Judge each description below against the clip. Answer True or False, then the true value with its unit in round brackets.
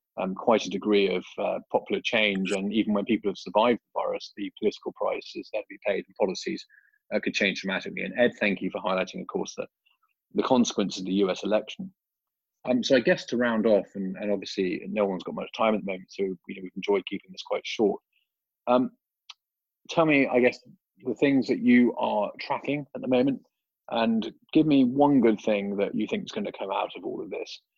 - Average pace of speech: False (220 wpm)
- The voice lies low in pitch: True (125 Hz)